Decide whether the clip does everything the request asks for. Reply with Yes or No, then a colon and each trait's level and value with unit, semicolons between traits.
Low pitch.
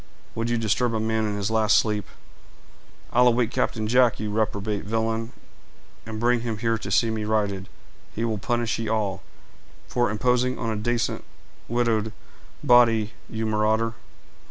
Yes: low, 110 Hz